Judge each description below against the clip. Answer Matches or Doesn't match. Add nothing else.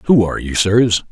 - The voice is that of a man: Matches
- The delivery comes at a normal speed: Doesn't match